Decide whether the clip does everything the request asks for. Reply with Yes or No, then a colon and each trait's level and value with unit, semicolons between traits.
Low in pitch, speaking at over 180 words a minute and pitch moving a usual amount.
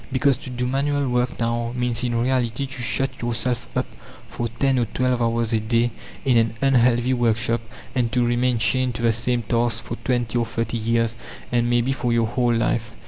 No: low, 120 Hz; average, 195 wpm; narrow, 1.5 semitones